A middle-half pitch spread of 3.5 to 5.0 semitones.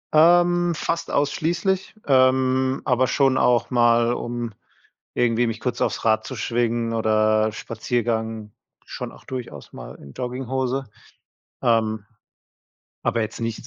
No: average, 2.7 semitones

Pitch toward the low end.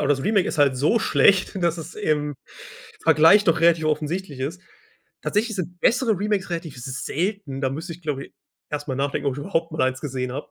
No: medium, 160 Hz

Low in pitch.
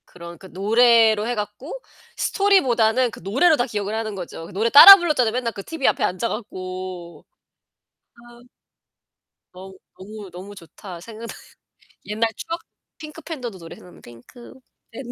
No: high, 220 Hz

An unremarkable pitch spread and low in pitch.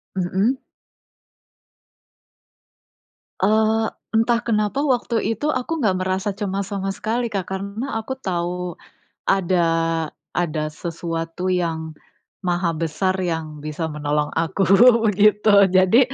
No: average, 4.2 semitones; medium, 185 Hz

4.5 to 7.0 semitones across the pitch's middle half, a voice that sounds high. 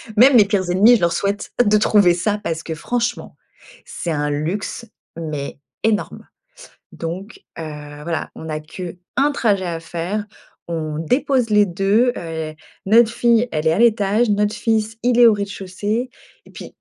Yes: average, 5.0 semitones; high, 200 Hz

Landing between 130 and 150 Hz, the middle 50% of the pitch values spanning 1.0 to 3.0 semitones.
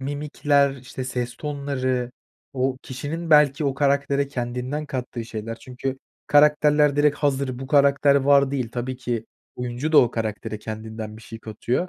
Yes: low, 135 Hz; average, 2.7 semitones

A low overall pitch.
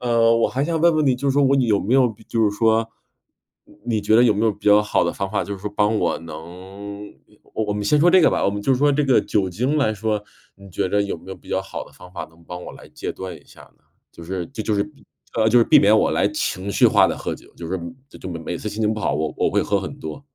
Yes: low, 105 Hz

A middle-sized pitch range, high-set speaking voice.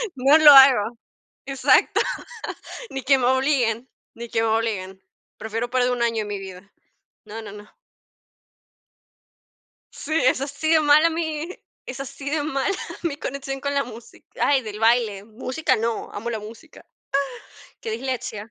Yes: average, 4.0 semitones; very high, 255 Hz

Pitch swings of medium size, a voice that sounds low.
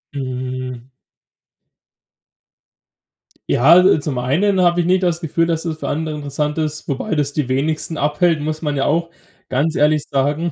No: average, 3.0 semitones; medium, 150 Hz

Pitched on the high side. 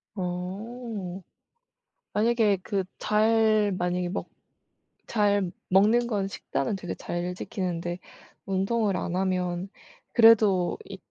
Yes: high, 195 Hz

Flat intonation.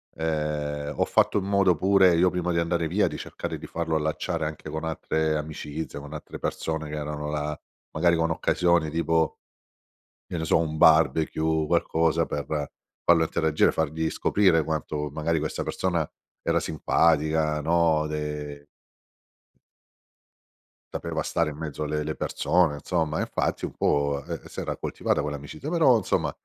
Yes: narrow, 1.7 semitones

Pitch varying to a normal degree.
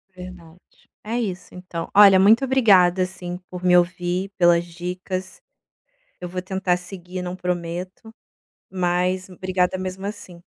No: narrow, 1.1 semitones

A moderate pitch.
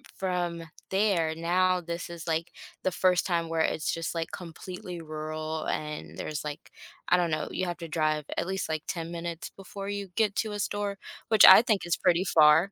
Yes: medium, 170 Hz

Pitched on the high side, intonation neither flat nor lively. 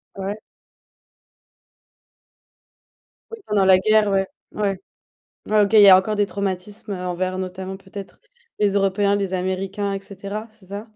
No: high, 195 Hz; narrow, 1.5 semitones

